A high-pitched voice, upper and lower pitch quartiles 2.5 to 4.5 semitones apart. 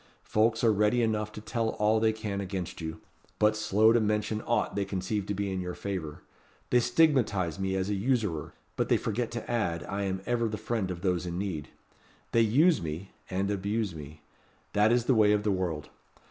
No: low, 105 Hz; average, 3.0 semitones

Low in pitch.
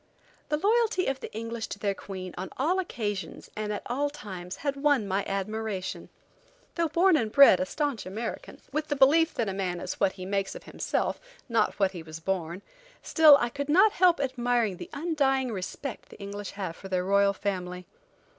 No: high, 220 Hz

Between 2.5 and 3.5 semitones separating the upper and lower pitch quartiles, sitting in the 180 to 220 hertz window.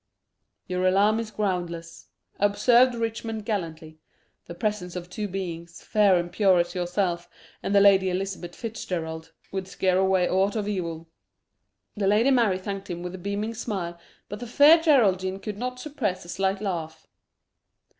Yes: average, 3.2 semitones; high, 190 Hz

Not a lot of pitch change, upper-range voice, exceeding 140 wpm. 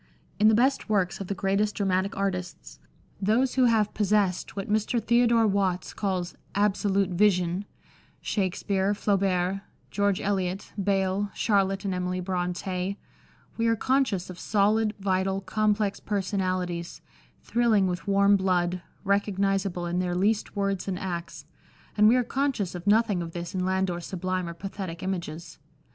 Yes: narrow, 2.2 semitones; high, 195 Hz; average, 155 wpm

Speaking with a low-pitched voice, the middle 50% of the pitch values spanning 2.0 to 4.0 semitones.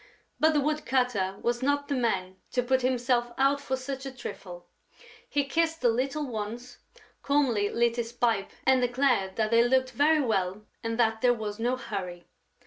No: high, 245 Hz; average, 3.3 semitones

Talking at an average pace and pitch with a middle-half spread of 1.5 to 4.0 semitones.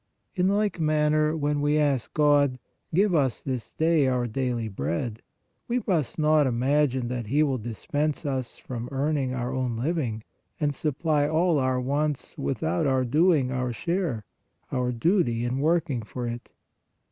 Yes: average, 160 wpm; average, 3.7 semitones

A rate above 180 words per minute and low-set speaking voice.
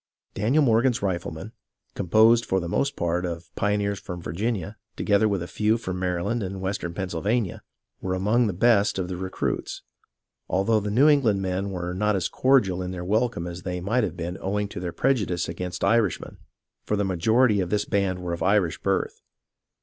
Yes: average, 190 wpm; very low, 95 Hz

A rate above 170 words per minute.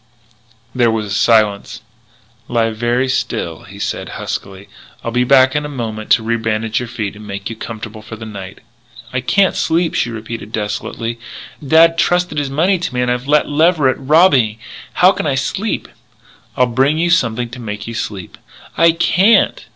Yes: average, 180 wpm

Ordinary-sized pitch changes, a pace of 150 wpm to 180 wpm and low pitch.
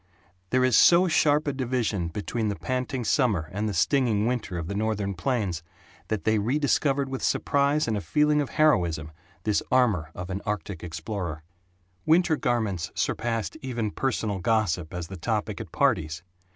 No: wide, 5.9 semitones; average, 165 wpm; low, 110 Hz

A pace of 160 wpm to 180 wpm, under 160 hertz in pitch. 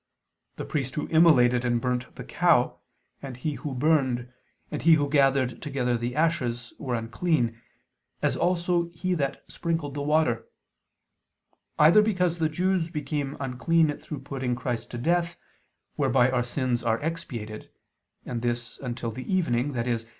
No: average, 150 wpm; low, 135 Hz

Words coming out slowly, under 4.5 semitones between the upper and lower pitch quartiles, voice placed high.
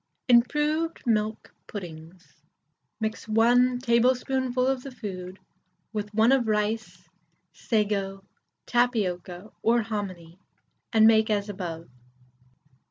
Yes: slow, 100 wpm; average, 3.9 semitones; high, 220 Hz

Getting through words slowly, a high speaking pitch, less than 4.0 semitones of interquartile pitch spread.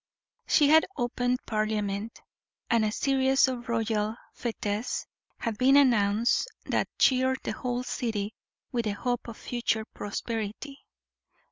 Yes: slow, 125 wpm; high, 235 Hz; average, 2.9 semitones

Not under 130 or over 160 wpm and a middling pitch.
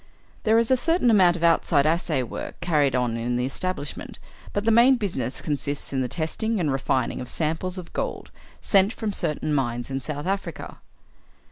No: average, 180 wpm; medium, 160 Hz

